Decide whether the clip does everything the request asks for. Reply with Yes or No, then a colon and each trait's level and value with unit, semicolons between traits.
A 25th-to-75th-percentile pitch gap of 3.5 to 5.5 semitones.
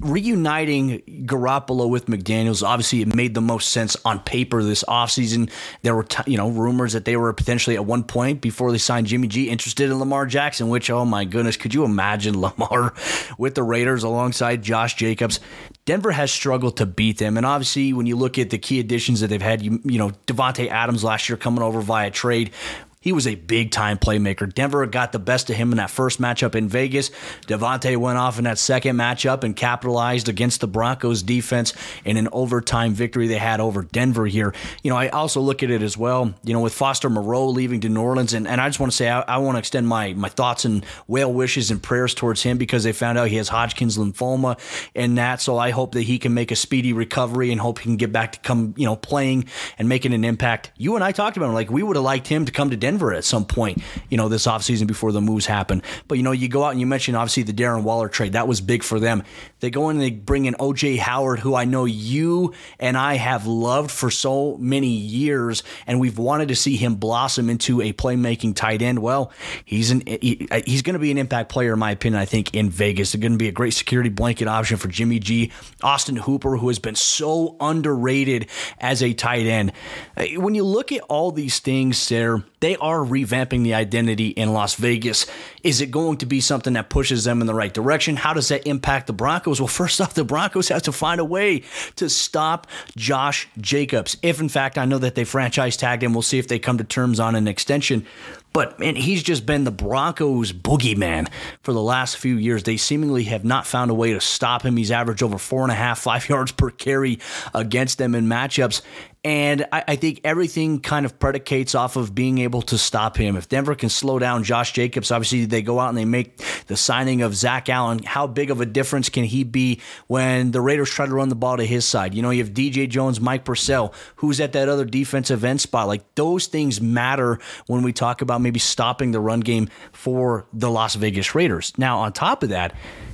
No: average, 2.8 semitones